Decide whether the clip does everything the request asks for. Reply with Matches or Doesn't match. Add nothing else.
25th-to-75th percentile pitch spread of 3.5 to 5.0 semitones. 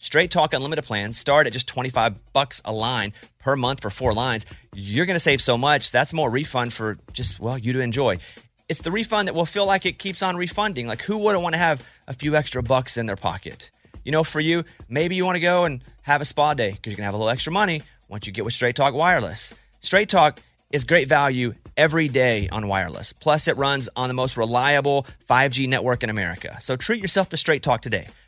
Doesn't match